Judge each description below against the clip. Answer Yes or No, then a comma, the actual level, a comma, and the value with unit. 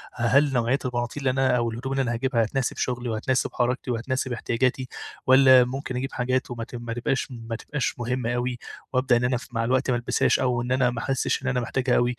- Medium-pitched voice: No, low, 125 Hz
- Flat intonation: Yes, narrow, 1.6 semitones